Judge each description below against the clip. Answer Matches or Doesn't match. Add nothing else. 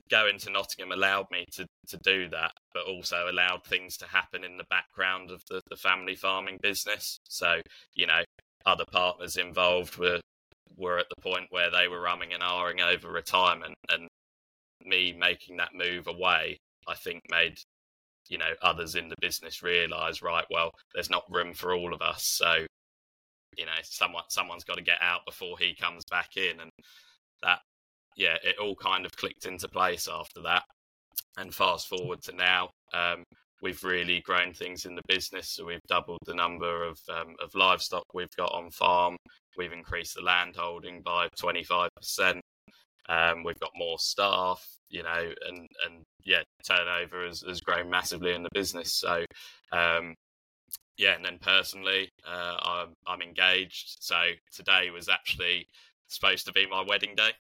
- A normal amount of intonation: Doesn't match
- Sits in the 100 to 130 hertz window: Doesn't match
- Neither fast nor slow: Matches